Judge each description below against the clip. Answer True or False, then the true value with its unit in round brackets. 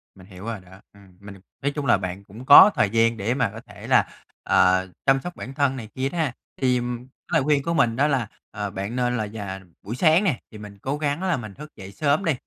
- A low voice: True (120 Hz)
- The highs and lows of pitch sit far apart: True (5.9 semitones)